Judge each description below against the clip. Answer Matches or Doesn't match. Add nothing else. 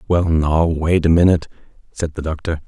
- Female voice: Doesn't match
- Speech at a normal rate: Matches